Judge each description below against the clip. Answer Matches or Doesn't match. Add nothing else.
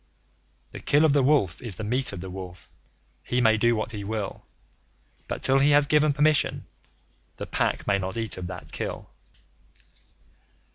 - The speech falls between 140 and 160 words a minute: Doesn't match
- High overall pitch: Doesn't match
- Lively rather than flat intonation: Matches